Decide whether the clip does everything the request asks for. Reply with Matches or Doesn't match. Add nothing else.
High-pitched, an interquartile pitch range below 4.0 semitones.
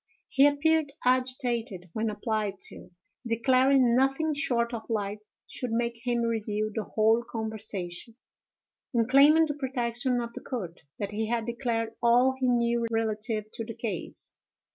Matches